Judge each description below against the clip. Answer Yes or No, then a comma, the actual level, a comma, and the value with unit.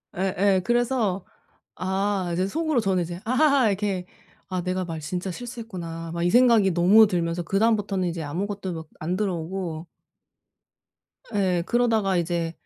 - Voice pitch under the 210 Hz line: Yes, high, 190 Hz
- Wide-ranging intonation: No, average, 3.5 semitones